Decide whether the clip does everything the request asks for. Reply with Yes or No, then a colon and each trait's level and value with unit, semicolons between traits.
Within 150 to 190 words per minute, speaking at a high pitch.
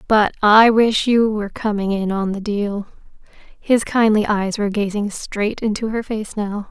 Yes: average, 170 wpm; high, 210 Hz